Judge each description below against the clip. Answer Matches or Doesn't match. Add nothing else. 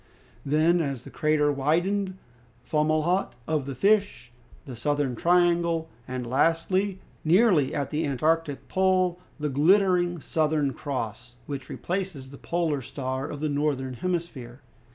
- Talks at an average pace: Doesn't match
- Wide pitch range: Doesn't match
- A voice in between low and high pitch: Matches